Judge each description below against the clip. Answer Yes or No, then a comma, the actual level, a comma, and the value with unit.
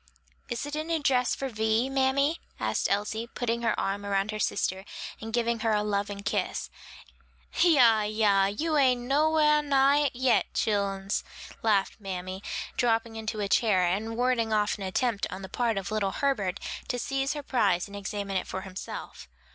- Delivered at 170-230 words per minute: Yes, average, 180 wpm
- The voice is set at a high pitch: Yes, high, 220 Hz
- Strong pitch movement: No, average, 4.5 semitones